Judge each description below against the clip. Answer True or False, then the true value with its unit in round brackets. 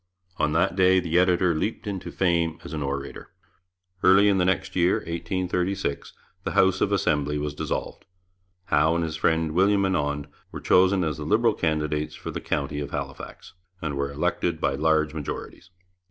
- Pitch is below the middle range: True (80 Hz)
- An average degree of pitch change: True (3.6 semitones)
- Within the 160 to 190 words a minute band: True (170 wpm)